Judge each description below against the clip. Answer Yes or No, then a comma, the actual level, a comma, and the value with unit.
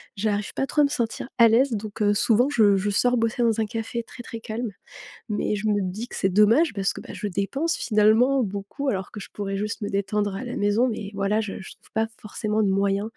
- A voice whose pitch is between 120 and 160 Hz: No, high, 215 Hz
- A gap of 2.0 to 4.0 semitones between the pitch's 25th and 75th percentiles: Yes, narrow, 2.6 semitones